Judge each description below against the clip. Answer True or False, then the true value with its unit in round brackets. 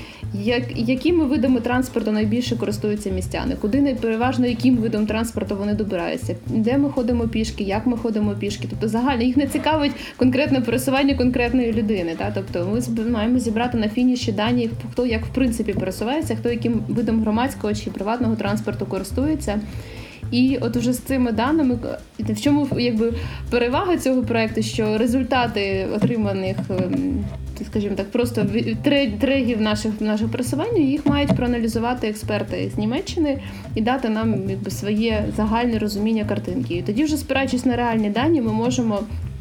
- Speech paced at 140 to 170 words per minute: True (145 wpm)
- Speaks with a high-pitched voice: True (235 Hz)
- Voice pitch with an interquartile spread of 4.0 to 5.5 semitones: False (3.3 semitones)